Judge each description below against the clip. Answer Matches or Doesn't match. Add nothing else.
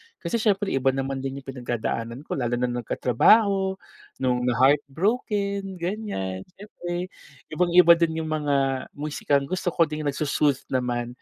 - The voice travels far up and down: Matches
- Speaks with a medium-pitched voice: Matches